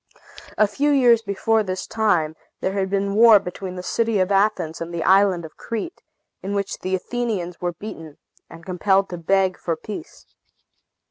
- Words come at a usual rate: Yes, average, 180 wpm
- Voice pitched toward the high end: Yes, high, 195 Hz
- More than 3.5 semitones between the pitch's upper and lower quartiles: No, average, 3.2 semitones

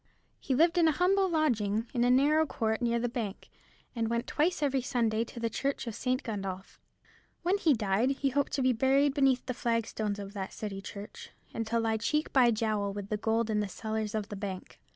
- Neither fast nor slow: No, fast, 215 wpm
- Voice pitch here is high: Yes, high, 235 Hz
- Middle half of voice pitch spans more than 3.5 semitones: Yes, average, 4.2 semitones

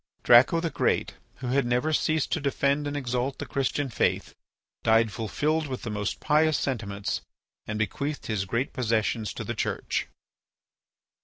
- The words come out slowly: No, average, 155 wpm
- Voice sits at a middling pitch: No, low, 130 Hz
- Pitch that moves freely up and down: No, average, 4.4 semitones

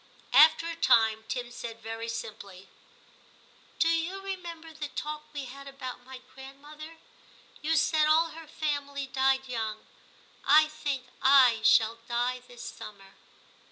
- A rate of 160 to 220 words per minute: No, average, 140 wpm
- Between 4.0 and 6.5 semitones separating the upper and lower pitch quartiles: Yes, average, 4.7 semitones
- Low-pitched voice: No, very high, 275 Hz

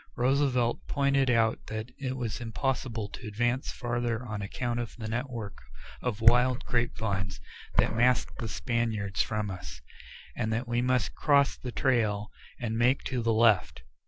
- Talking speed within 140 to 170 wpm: Yes, average, 160 wpm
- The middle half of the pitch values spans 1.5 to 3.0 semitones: Yes, narrow, 2.4 semitones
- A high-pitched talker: No, low, 120 Hz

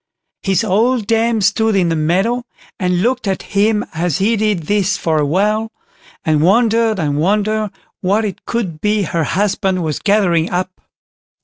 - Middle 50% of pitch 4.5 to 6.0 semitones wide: No, average, 3.8 semitones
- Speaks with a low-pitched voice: No, high, 200 Hz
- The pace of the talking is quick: No, average, 165 wpm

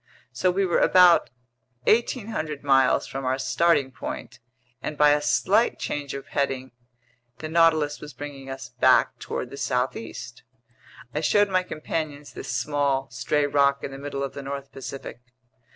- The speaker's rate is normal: Yes, average, 155 wpm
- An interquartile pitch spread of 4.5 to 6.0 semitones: No, average, 2.7 semitones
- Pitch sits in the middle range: Yes, medium, 145 Hz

